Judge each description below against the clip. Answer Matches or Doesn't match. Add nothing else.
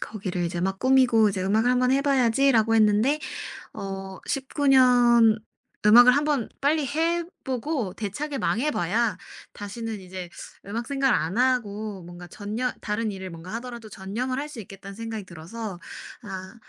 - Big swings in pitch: Doesn't match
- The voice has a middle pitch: Doesn't match